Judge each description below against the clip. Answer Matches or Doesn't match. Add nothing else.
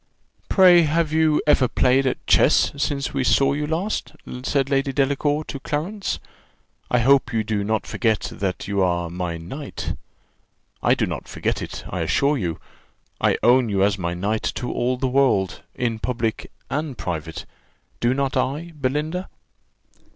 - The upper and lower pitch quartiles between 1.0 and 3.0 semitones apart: Doesn't match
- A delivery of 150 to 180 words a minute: Matches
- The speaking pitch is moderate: Doesn't match